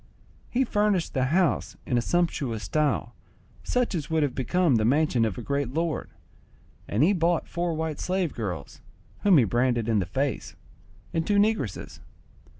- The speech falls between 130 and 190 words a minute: Yes, average, 165 wpm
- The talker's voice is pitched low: No, medium, 150 Hz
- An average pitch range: No, wide, 6.3 semitones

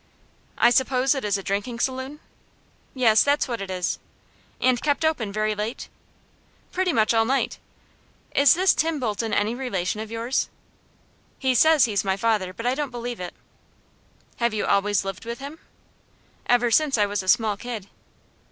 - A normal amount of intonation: Yes, average, 4.1 semitones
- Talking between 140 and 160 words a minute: No, average, 170 wpm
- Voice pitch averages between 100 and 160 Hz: No, high, 235 Hz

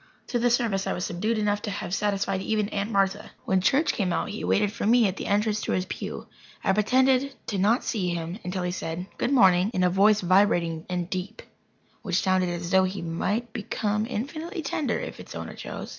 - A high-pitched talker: Yes, high, 200 Hz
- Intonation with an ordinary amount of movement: Yes, average, 3.2 semitones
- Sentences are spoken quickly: Yes, fast, 215 wpm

